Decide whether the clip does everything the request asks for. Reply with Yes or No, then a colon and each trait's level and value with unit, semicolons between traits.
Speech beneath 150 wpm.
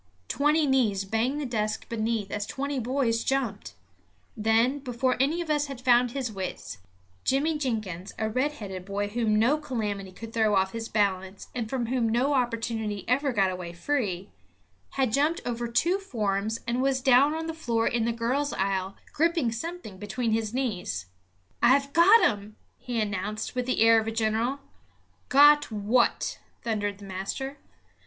No: average, 165 wpm